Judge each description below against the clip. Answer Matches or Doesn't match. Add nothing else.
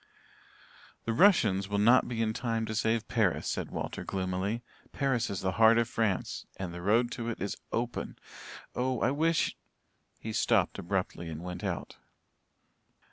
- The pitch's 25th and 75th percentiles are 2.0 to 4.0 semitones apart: Matches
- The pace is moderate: Matches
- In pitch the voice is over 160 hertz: Doesn't match